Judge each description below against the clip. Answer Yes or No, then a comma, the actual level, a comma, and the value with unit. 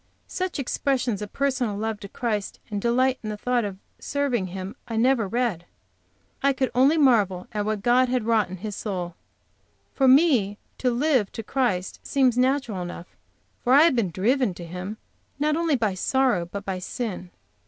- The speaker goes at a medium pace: Yes, average, 180 wpm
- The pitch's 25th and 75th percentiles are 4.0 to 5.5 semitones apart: Yes, average, 4.8 semitones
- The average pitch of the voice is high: Yes, high, 230 Hz